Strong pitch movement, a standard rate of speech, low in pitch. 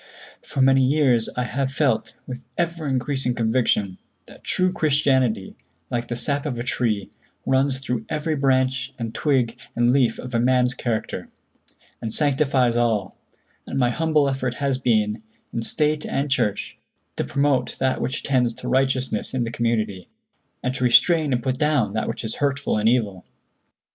No: average, 2.8 semitones; average, 165 wpm; low, 130 Hz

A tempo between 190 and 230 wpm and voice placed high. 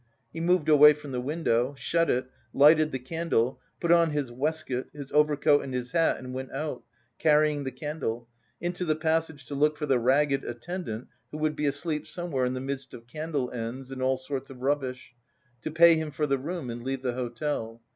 No: fast, 205 wpm; medium, 145 Hz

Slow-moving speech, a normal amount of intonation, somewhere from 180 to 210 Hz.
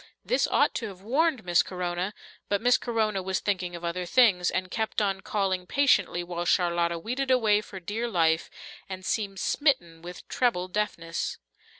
No: average, 170 wpm; average, 4.1 semitones; high, 190 Hz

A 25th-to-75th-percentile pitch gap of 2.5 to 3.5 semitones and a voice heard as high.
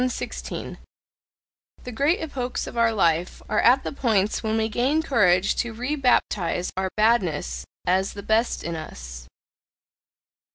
No: wide, 5.5 semitones; high, 220 Hz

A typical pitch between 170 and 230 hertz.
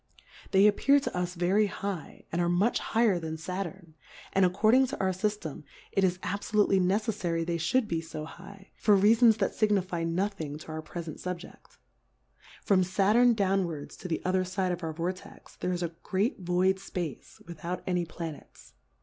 Yes: medium, 185 Hz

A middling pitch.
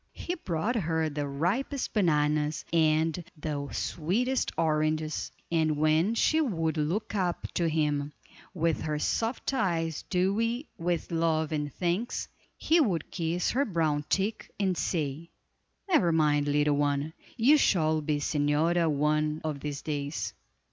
Yes: medium, 160 Hz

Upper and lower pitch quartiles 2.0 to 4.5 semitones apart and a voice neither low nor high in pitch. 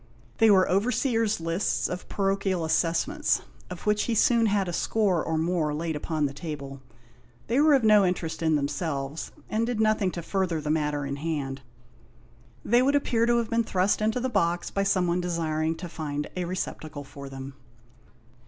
No: wide, 5.5 semitones; medium, 175 Hz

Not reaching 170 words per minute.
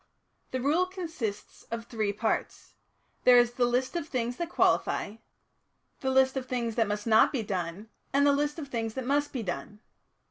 No: average, 185 wpm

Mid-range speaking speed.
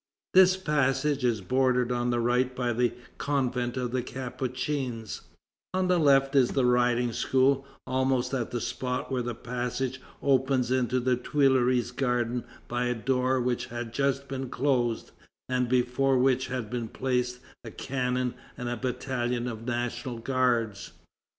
Yes: average, 150 wpm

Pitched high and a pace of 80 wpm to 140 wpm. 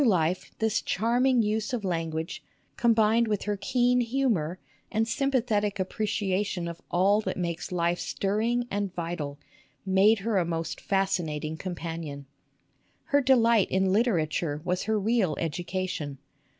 Yes: high, 195 Hz; slow, 135 wpm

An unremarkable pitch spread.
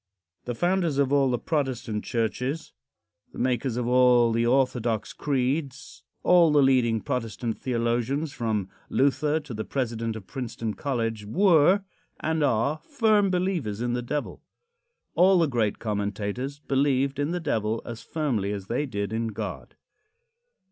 Yes: average, 4.4 semitones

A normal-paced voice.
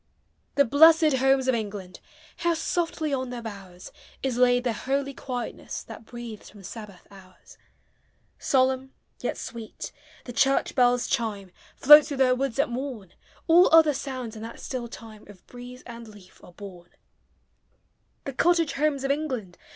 Yes: average, 155 wpm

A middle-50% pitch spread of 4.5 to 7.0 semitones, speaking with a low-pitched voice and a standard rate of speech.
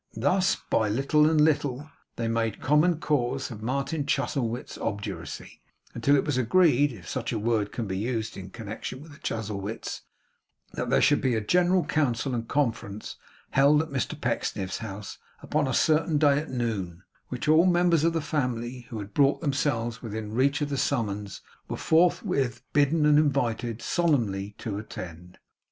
Yes: average, 5.0 semitones; low, 130 Hz; average, 170 wpm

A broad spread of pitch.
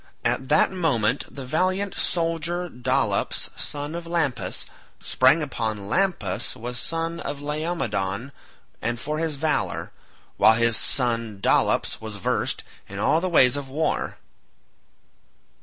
Yes: wide, 5.9 semitones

